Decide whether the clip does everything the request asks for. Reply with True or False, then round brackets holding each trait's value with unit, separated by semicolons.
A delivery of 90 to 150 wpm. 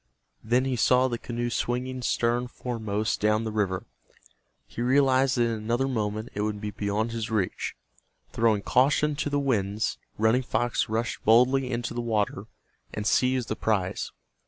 False (160 wpm)